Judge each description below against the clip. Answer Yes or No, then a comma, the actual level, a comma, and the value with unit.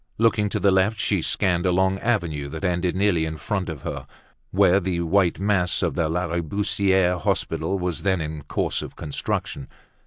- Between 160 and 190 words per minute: Yes, average, 180 wpm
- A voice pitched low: Yes, very low, 90 Hz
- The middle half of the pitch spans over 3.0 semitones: No, narrow, 2.6 semitones